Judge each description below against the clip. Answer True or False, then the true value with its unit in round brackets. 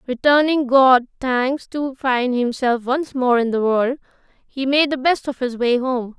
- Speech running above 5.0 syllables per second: False (4.1 syllables/s)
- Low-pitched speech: False (260 Hz)